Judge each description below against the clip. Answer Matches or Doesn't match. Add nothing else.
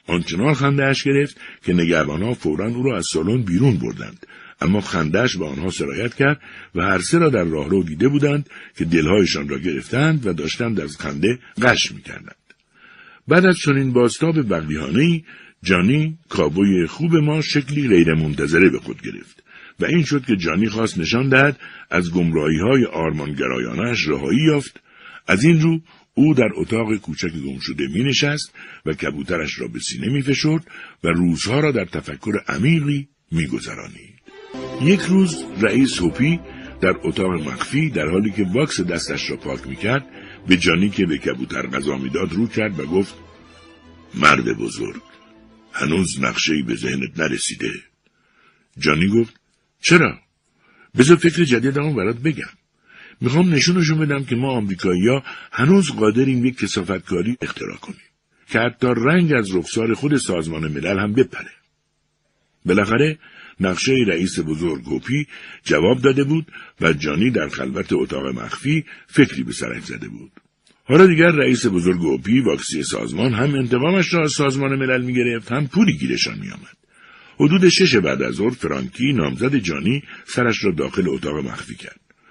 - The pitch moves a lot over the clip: Matches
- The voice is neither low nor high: Doesn't match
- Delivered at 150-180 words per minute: Matches